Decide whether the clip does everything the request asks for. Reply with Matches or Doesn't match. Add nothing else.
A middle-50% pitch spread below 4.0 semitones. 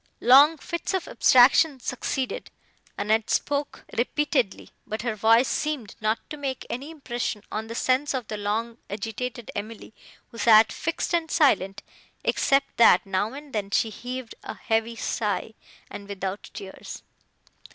Doesn't match